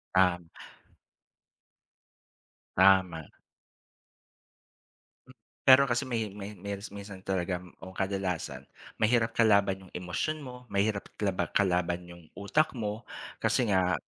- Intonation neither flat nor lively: Yes, average, 3.3 semitones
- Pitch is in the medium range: No, low, 100 Hz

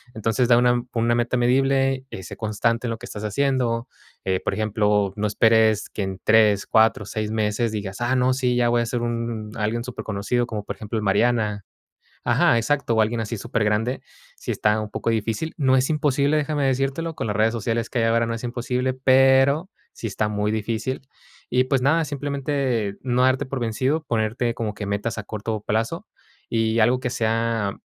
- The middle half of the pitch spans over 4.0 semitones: No, average, 3.0 semitones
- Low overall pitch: Yes, low, 115 Hz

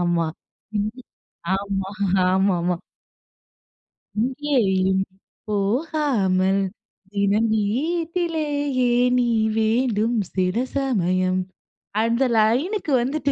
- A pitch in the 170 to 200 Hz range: No, high, 220 Hz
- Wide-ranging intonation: Yes, wide, 6.4 semitones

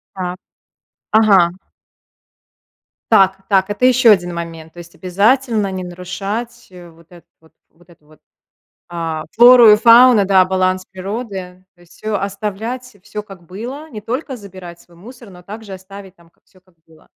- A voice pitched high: Yes, high, 195 Hz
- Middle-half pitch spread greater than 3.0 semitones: Yes, average, 3.7 semitones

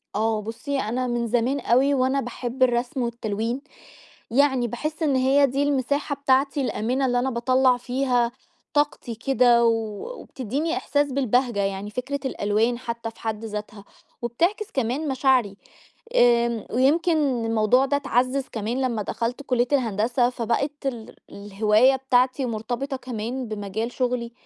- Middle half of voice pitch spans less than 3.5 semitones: Yes, average, 2.8 semitones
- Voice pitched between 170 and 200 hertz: No, high, 245 Hz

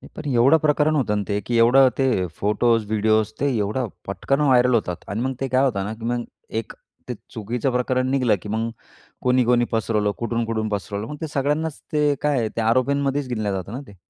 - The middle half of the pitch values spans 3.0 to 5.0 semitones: Yes, average, 3.6 semitones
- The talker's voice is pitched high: No, low, 120 Hz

